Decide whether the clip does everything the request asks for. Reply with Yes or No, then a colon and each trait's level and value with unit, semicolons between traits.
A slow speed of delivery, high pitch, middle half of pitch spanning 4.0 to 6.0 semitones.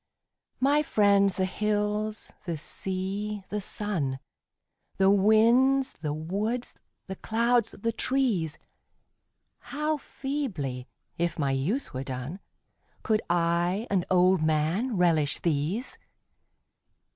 Yes: slow, 105 wpm; high, 195 Hz; average, 5.2 semitones